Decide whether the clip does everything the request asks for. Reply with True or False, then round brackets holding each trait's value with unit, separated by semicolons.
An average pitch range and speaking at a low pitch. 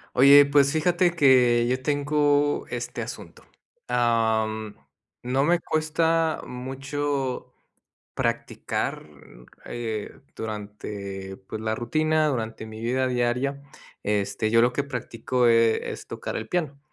True (4.4 semitones; 125 Hz)